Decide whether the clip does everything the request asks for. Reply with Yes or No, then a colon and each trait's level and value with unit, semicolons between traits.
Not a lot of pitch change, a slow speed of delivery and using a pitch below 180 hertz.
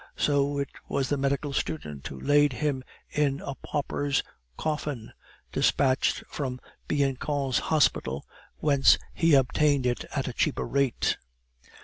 Yes: narrow, 1.9 semitones; slow, 125 wpm; medium, 140 Hz